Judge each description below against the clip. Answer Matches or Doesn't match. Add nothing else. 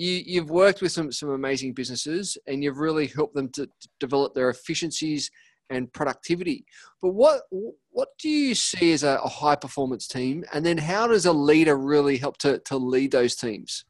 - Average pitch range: Matches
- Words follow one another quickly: Doesn't match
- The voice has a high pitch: Doesn't match